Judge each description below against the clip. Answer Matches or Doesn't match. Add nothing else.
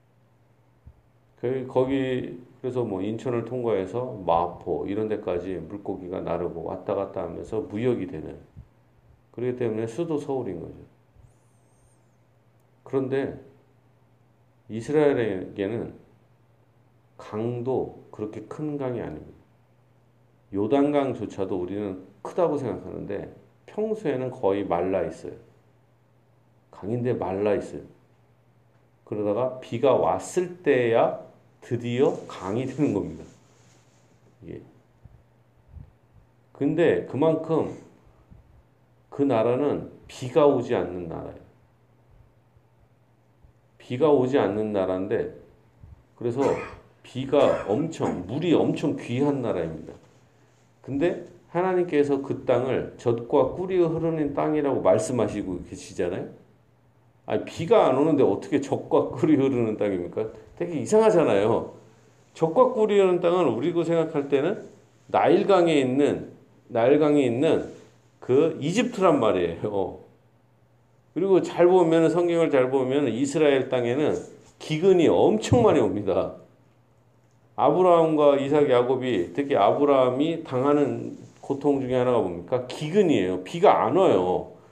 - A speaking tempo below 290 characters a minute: Matches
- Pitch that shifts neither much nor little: Matches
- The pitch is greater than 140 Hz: Doesn't match